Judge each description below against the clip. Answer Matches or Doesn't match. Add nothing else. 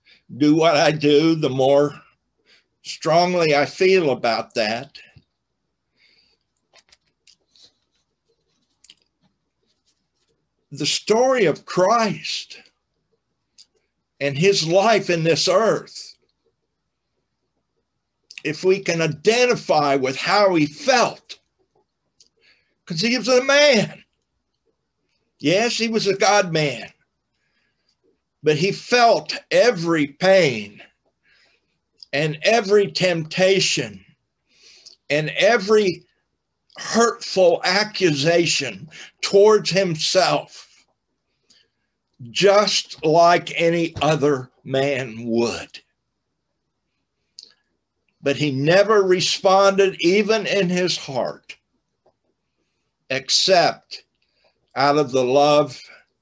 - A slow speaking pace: Matches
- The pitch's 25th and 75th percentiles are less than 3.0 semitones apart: Doesn't match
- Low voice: Doesn't match